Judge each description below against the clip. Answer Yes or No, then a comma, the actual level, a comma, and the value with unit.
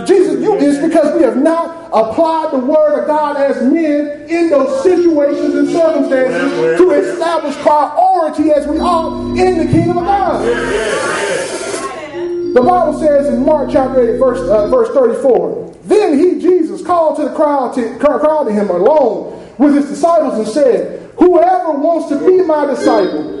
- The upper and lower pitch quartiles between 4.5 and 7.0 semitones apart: No, average, 3.3 semitones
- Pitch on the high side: Yes, very high, 310 Hz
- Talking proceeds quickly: No, average, 165 wpm